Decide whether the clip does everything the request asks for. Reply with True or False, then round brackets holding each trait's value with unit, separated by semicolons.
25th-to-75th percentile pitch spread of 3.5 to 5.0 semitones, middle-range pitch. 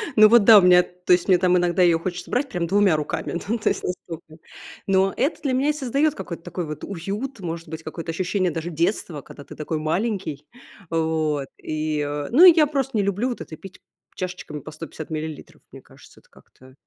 True (4.5 semitones; 180 Hz)